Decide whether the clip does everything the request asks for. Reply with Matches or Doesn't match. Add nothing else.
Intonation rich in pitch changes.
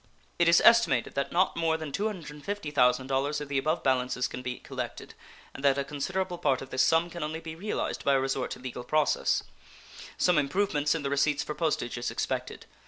Doesn't match